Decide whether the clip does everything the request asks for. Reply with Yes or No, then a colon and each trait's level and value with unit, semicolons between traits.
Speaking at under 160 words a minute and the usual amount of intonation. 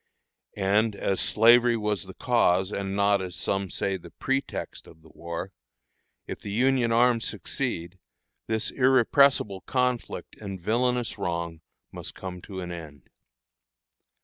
Yes: slow, 135 wpm; average, 4.6 semitones